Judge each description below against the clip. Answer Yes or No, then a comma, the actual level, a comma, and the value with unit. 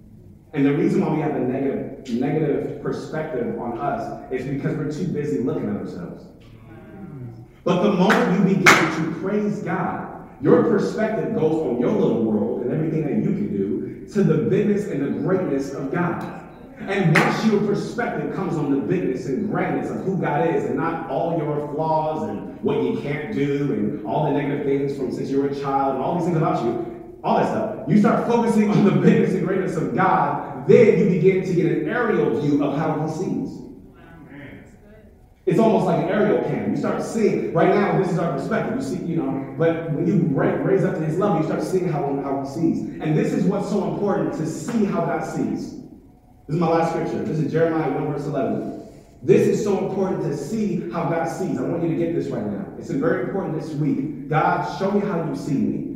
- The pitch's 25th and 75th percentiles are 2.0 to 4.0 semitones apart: No, average, 4.8 semitones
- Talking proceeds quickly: Yes, fast, 215 wpm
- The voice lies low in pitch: No, medium, 165 Hz